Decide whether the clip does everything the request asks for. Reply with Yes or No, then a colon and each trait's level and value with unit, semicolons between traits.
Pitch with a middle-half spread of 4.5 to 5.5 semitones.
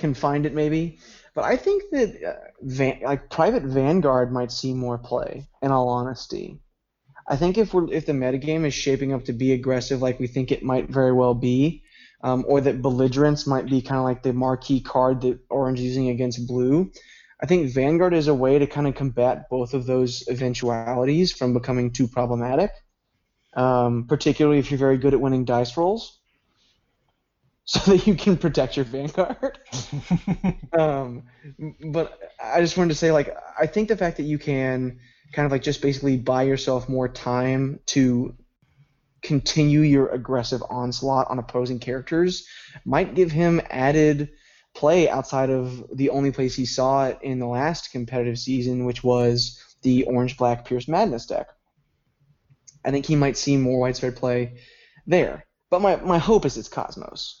No: average, 3.0 semitones